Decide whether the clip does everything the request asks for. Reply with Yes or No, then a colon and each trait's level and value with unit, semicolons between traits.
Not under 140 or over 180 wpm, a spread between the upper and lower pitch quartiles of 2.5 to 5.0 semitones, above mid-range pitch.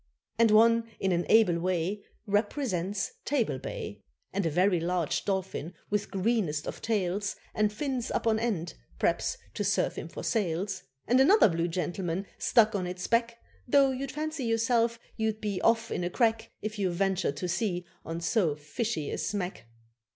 Yes: average, 170 wpm; average, 4.4 semitones; high, 205 Hz